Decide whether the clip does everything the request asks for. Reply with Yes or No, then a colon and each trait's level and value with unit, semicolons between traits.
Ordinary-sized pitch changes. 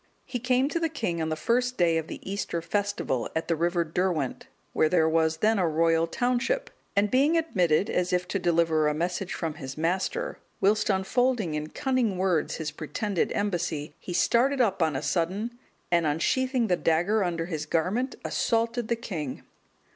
No: wide, 6.1 semitones